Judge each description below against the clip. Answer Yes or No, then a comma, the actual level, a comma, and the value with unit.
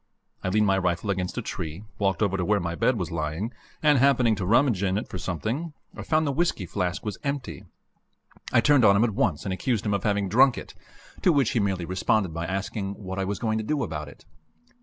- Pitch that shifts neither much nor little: Yes, average, 4.4 semitones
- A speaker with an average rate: No, fast, 235 wpm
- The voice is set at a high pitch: No, low, 100 Hz